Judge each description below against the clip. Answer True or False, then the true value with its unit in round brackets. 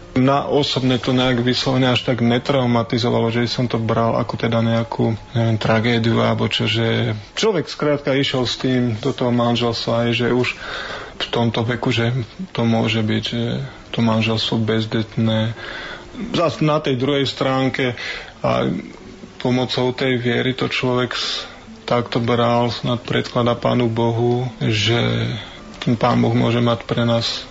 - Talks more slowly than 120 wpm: False (145 wpm)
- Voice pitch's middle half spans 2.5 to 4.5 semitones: False (1.9 semitones)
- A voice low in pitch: True (120 Hz)